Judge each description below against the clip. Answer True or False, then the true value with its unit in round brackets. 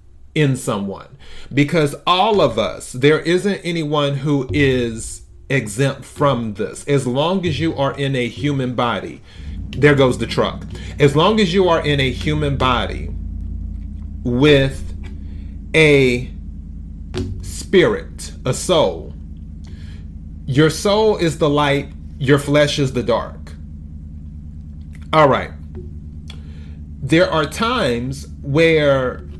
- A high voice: False (110 Hz)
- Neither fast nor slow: False (115 wpm)